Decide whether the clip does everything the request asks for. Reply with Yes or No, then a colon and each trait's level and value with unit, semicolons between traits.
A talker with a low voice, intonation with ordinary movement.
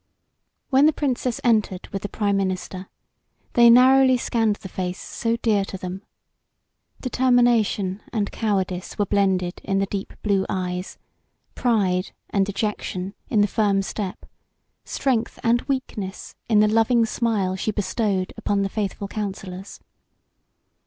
No: high, 205 Hz; average, 3.3 semitones